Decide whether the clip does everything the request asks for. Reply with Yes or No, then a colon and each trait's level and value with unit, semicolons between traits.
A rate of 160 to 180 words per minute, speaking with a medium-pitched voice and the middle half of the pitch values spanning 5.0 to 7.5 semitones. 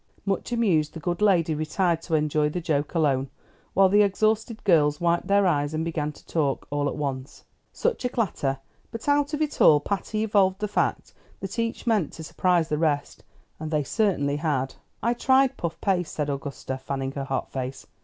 No: average, 195 wpm; medium, 165 Hz; wide, 5.6 semitones